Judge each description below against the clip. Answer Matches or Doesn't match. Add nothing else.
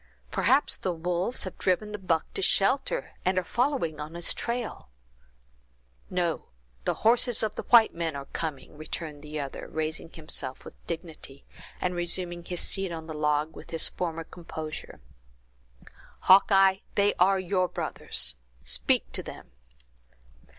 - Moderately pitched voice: Matches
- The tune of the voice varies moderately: Matches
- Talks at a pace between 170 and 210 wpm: Doesn't match